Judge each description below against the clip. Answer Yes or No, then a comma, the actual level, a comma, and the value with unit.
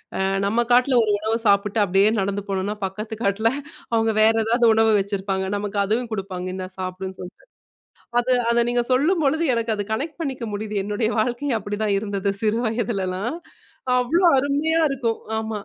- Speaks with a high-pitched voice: Yes, high, 220 Hz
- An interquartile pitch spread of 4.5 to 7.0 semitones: No, average, 3.3 semitones